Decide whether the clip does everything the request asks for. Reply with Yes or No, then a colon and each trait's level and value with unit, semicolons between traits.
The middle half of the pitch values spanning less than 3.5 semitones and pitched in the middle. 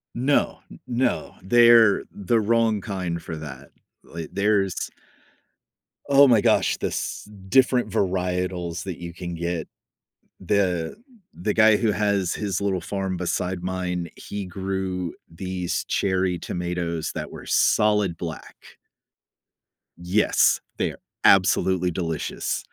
No: average, 2.9 semitones; very low, 95 Hz